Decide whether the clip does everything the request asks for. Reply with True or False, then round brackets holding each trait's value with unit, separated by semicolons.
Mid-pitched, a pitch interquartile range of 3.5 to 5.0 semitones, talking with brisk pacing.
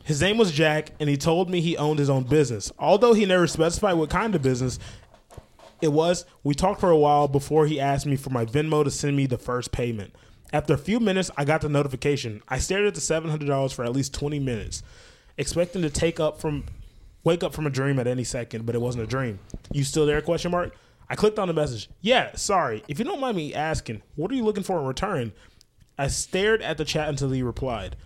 True (150 Hz; 4.5 semitones; 235 wpm)